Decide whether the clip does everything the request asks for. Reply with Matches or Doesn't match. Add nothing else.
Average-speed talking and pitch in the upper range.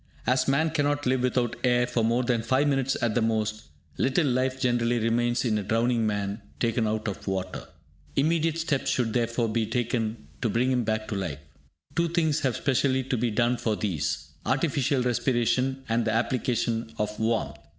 Doesn't match